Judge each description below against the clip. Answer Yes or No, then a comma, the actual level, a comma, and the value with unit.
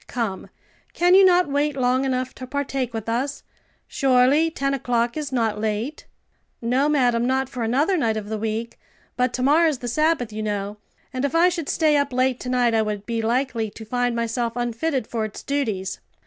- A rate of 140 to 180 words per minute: No, average, 195 wpm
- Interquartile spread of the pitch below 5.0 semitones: Yes, average, 3.7 semitones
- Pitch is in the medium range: No, very high, 250 Hz